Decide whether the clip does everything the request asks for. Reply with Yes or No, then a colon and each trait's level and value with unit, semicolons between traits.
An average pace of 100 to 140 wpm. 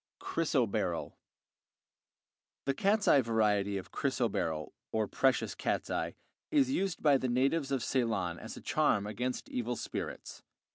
Yes: slow, 135 wpm